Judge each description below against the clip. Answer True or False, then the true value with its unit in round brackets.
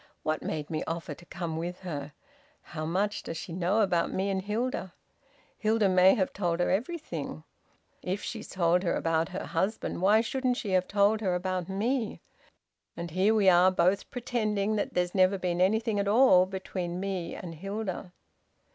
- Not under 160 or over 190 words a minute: True (175 wpm)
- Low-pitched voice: False (190 Hz)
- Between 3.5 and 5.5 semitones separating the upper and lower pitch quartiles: False (3.1 semitones)